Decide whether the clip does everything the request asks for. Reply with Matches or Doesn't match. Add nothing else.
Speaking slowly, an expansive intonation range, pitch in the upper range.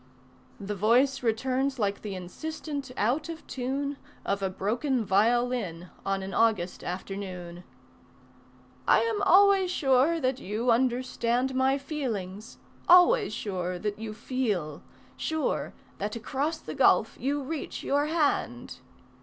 Matches